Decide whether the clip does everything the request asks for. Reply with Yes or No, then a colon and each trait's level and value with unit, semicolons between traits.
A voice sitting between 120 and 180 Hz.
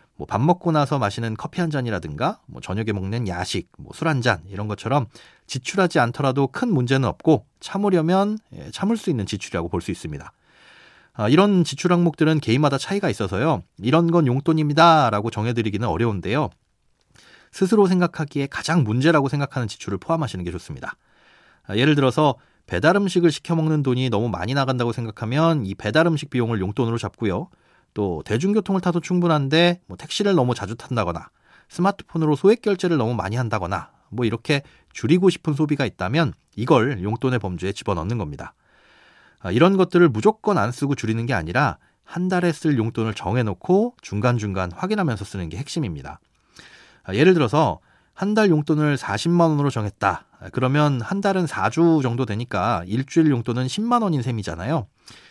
Yes: low, 135 Hz